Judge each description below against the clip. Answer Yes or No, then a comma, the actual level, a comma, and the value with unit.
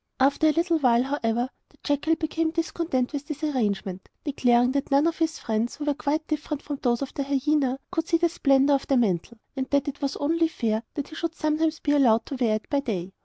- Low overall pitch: No, very high, 280 Hz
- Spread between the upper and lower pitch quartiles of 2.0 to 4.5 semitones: Yes, average, 4.0 semitones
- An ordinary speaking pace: No, fast, 230 wpm